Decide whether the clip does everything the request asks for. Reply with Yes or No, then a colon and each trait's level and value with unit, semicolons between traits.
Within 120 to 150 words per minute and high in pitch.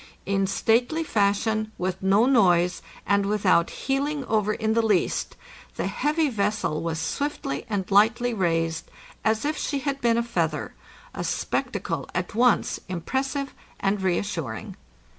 Yes: average, 145 wpm; high, 210 Hz